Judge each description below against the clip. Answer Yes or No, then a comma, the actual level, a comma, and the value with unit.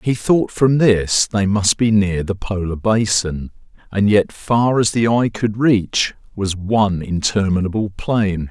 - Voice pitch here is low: Yes, low, 105 Hz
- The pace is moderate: Yes, average, 160 wpm